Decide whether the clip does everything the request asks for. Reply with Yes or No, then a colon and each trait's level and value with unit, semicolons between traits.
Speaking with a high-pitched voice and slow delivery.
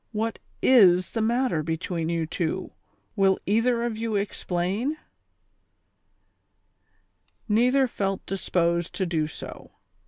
Yes: high, 195 Hz; slow, 115 wpm